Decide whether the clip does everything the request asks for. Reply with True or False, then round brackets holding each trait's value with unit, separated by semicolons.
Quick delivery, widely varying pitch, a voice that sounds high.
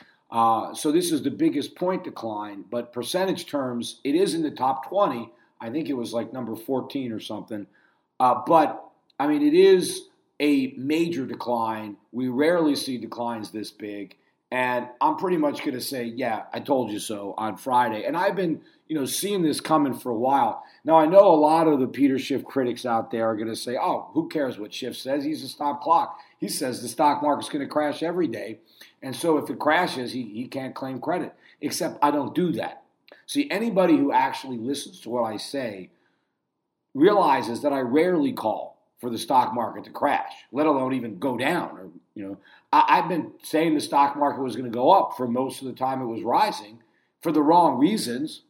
False (210 wpm; 6.4 semitones; 140 Hz)